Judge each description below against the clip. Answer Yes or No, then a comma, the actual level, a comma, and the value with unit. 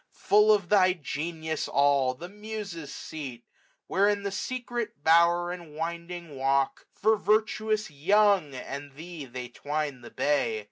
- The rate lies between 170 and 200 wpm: No, average, 145 wpm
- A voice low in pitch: No, medium, 170 Hz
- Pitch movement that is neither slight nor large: No, wide, 6.0 semitones